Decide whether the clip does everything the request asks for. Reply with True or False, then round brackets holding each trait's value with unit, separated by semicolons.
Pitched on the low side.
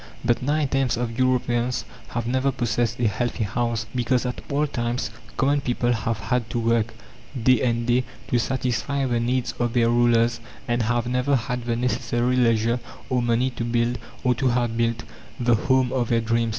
True (120 Hz)